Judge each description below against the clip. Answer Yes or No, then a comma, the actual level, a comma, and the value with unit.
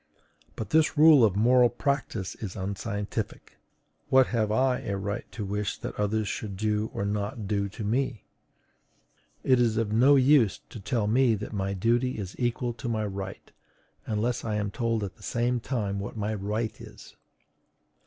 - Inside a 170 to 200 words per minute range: Yes, average, 175 wpm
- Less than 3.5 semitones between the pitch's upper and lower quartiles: Yes, average, 3.0 semitones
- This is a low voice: Yes, low, 110 Hz